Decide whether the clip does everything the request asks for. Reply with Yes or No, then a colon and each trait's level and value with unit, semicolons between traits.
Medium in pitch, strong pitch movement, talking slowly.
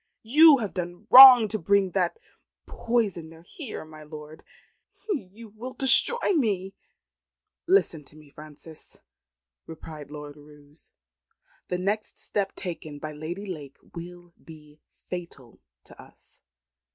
Yes: medium, 175 Hz; wide, 5.8 semitones; slow, 120 wpm